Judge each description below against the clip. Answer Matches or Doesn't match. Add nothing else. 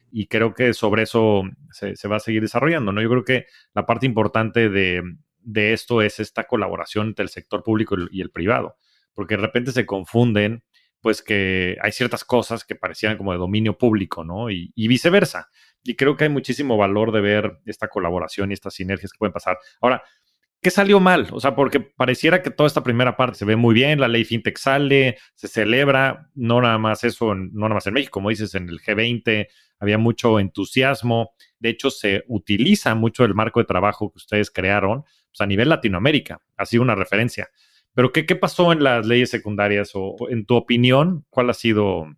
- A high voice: Doesn't match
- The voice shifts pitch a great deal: Doesn't match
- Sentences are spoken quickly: Matches